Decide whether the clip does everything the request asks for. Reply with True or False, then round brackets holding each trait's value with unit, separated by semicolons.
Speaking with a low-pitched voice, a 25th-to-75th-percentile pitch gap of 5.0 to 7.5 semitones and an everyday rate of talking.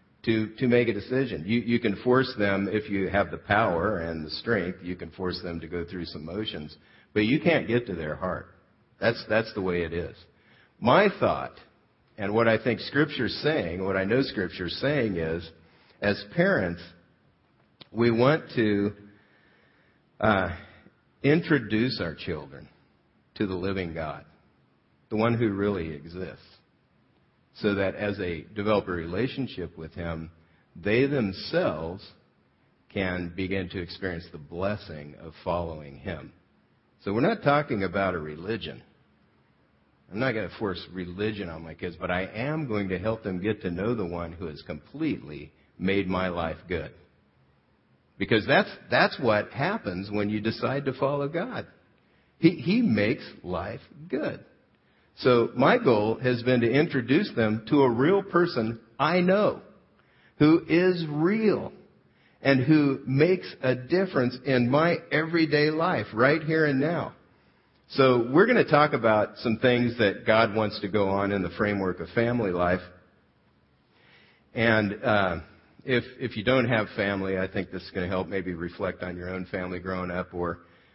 True (100 Hz; 5.5 semitones; 160 wpm)